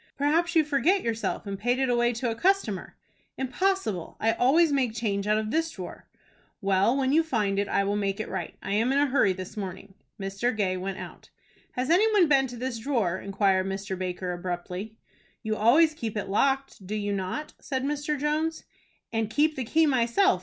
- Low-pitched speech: No, high, 230 Hz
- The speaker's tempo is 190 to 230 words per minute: Yes, average, 200 wpm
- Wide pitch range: Yes, wide, 6.4 semitones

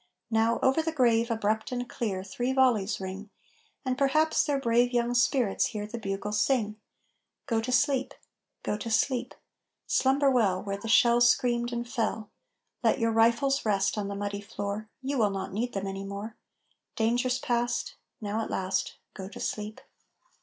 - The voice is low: No, high, 230 Hz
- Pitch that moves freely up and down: No, average, 3.3 semitones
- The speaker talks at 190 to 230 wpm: No, average, 165 wpm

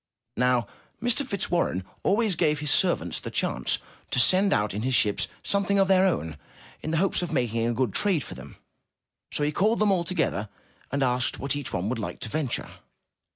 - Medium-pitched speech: Yes, medium, 150 Hz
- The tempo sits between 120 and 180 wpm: No, average, 195 wpm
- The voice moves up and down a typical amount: No, wide, 8.1 semitones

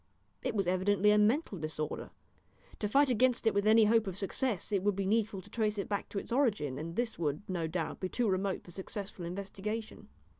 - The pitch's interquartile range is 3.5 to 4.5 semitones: No, average, 3.1 semitones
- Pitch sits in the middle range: No, high, 200 Hz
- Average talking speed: No, fast, 215 wpm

